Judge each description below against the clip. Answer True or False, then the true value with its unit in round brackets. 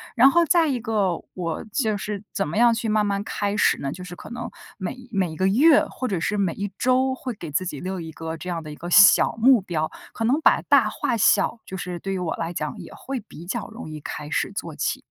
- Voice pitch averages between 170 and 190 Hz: False (200 Hz)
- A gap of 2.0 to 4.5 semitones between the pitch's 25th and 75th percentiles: False (5.3 semitones)